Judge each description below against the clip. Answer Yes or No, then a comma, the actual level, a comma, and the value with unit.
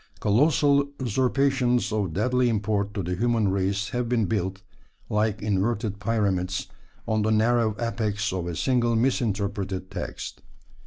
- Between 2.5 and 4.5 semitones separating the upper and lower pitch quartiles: Yes, average, 3.3 semitones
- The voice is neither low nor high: No, low, 110 Hz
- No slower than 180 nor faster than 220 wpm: No, slow, 135 wpm